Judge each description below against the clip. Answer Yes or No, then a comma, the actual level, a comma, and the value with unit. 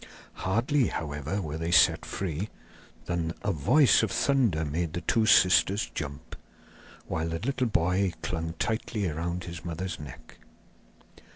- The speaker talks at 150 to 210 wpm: No, slow, 135 wpm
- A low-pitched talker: Yes, very low, 85 Hz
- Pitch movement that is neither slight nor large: Yes, average, 4.1 semitones